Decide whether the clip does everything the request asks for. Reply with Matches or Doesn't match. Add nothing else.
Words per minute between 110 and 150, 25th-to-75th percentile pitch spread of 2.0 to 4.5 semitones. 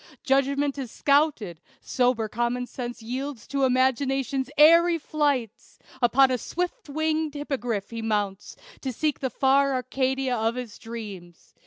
Matches